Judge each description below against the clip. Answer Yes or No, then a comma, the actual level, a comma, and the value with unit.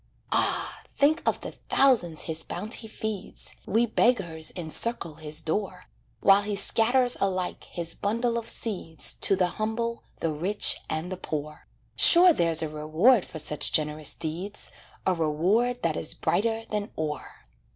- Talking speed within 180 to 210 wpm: No, average, 150 wpm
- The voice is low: No, high, 190 Hz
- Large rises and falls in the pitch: Yes, wide, 6.0 semitones